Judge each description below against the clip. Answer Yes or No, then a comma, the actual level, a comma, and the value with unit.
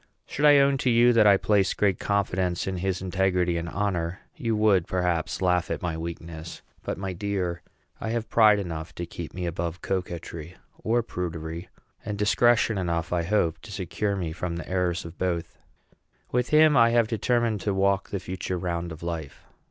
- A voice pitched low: Yes, very low, 95 Hz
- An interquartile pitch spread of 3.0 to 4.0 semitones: Yes, average, 3.6 semitones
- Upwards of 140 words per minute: Yes, average, 185 wpm